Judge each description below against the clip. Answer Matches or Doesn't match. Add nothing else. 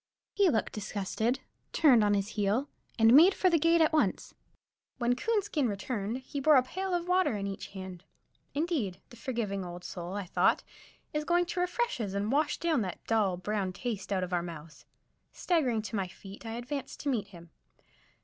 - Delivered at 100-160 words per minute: Doesn't match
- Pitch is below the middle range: Doesn't match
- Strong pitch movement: Matches